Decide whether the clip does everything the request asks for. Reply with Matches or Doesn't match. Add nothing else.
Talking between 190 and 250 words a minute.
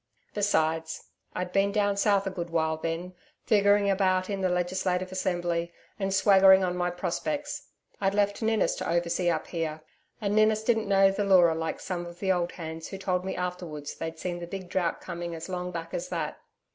Matches